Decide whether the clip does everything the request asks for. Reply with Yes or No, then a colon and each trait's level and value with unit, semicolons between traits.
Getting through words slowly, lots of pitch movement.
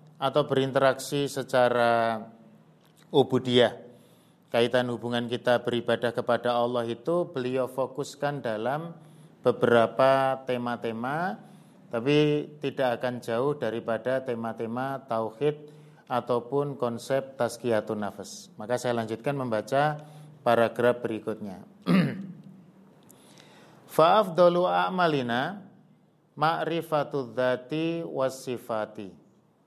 No: slow, 75 wpm; average, 4.0 semitones